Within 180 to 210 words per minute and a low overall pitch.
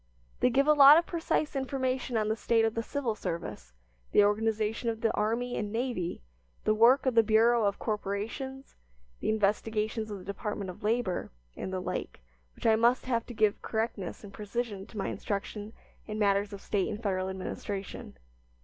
No: average, 185 wpm; high, 220 Hz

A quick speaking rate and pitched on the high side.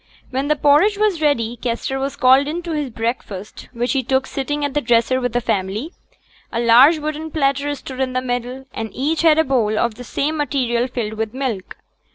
Yes: fast, 210 wpm; very high, 260 Hz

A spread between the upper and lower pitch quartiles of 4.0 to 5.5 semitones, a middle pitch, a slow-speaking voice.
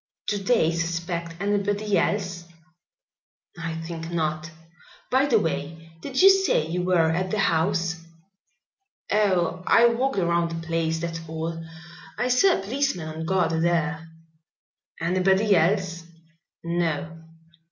No: average, 3.5 semitones; medium, 170 Hz; slow, 125 wpm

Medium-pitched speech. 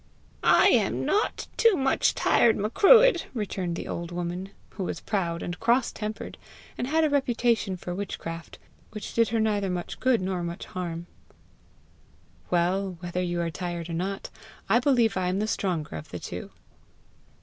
No: high, 195 Hz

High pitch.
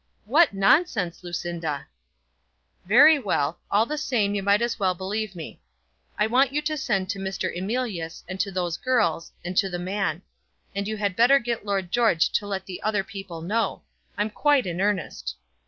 Yes: high, 200 Hz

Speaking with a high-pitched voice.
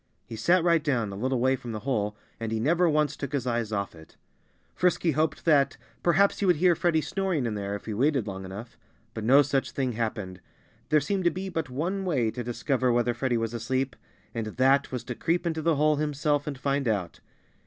No: low, 135 Hz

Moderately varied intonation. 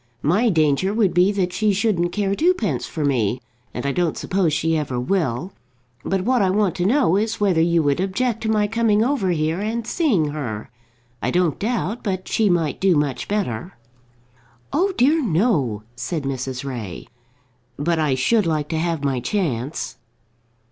No: wide, 6.1 semitones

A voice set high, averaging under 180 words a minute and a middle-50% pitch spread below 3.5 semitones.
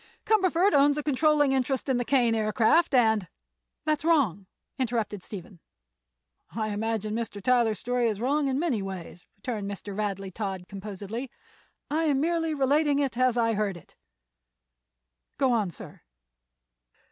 No: high, 235 Hz; average, 145 wpm; wide, 5.5 semitones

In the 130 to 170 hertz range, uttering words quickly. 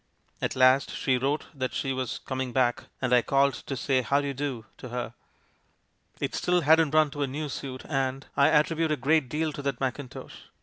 Yes: low, 135 Hz; fast, 225 wpm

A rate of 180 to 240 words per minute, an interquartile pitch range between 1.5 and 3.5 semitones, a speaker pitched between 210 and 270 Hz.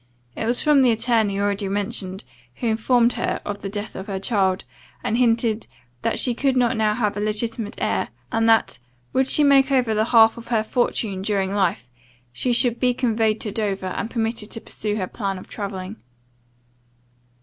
Yes: average, 185 wpm; average, 2.9 semitones; high, 220 Hz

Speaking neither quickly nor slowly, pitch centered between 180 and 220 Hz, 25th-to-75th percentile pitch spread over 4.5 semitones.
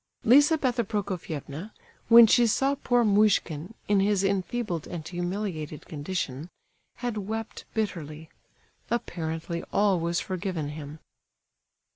No: slow, 105 wpm; high, 190 Hz; wide, 5.4 semitones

